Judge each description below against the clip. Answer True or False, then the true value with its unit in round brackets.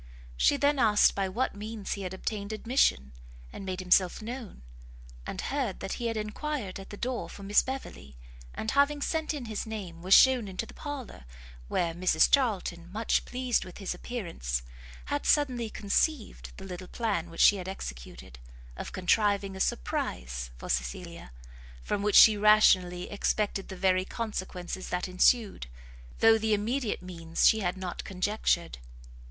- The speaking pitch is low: False (200 Hz)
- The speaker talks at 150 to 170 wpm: True (160 wpm)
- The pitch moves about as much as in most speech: True (4.0 semitones)